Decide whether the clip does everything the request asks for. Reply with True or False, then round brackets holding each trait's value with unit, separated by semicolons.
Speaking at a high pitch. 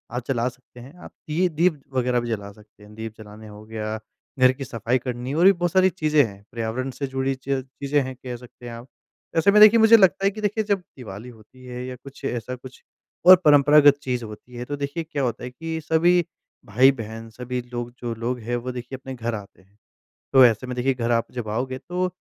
False (125 Hz)